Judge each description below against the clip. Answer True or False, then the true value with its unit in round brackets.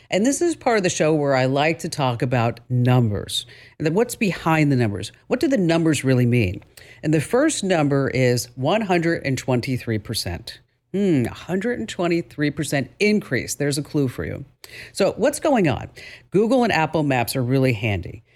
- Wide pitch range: True (6.4 semitones)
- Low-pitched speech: False (145 Hz)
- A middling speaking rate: True (165 wpm)